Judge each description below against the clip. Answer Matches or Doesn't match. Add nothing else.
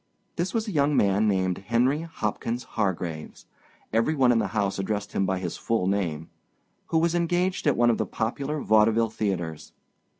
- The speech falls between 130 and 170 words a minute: Matches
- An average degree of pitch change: Doesn't match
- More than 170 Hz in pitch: Doesn't match